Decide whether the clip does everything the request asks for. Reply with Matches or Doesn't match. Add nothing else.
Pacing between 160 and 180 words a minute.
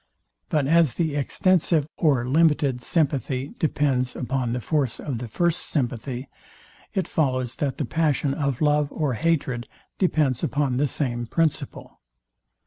Doesn't match